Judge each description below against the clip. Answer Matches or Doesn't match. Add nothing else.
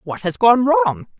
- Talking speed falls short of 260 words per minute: Matches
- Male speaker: Doesn't match